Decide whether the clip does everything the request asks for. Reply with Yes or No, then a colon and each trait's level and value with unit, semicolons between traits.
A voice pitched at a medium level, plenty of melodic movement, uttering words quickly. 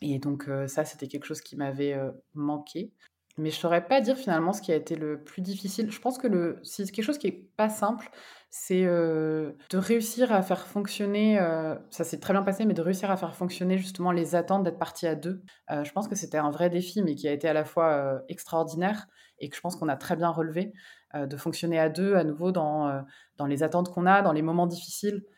No: medium, 175 Hz; average, 3.9 semitones; fast, 250 wpm